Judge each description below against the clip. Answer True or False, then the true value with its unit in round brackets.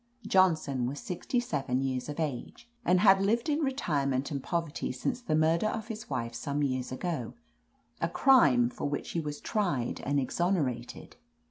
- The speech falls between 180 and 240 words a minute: False (165 wpm)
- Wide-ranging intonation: True (6.6 semitones)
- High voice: False (150 Hz)